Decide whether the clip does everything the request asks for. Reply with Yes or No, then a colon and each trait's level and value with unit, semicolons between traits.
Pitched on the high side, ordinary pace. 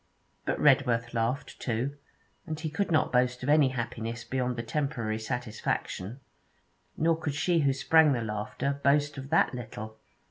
No: low, 130 Hz; average, 155 wpm